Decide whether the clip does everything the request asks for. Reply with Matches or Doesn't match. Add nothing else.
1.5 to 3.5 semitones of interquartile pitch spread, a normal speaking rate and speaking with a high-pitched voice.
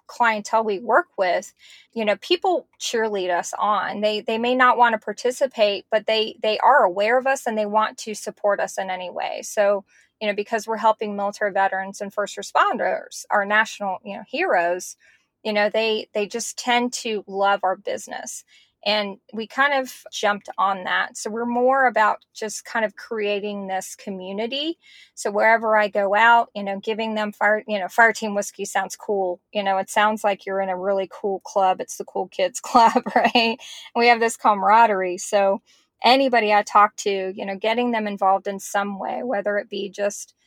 Matches